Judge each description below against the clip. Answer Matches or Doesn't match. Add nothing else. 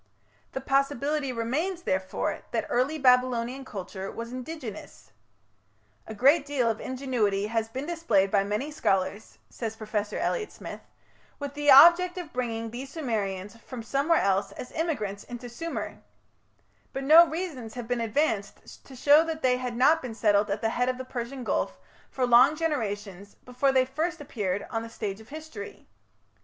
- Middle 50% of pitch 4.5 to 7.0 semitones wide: Matches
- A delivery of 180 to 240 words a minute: Doesn't match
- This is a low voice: Doesn't match